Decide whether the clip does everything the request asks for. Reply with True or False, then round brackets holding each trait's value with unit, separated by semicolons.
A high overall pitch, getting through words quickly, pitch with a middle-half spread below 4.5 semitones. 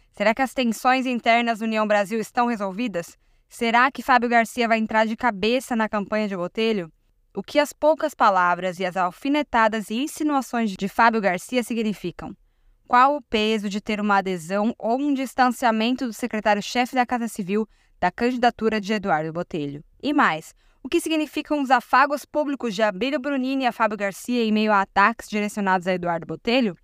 False (225 Hz; 175 wpm; 3.7 semitones)